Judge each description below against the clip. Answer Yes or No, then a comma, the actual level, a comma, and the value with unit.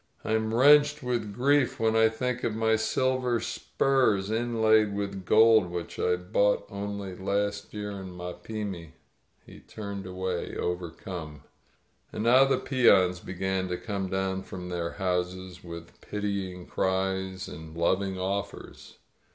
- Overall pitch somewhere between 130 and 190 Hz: No, low, 100 Hz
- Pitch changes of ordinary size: Yes, average, 3.4 semitones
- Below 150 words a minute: Yes, average, 140 wpm